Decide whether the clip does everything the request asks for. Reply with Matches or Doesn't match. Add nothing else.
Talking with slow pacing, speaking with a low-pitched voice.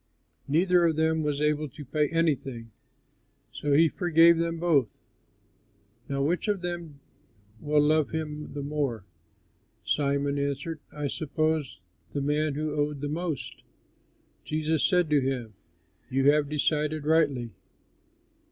Doesn't match